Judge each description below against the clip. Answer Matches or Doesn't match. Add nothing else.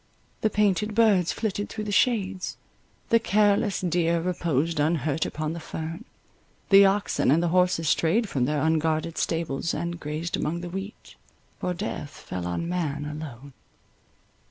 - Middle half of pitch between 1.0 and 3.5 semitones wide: Doesn't match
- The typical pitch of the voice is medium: Matches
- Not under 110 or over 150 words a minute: Matches